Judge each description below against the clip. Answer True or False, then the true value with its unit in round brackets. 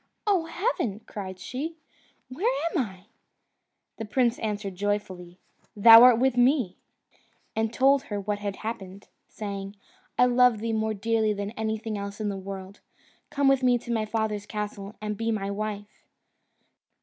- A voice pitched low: False (215 Hz)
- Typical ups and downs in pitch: True (3.2 semitones)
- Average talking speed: True (155 wpm)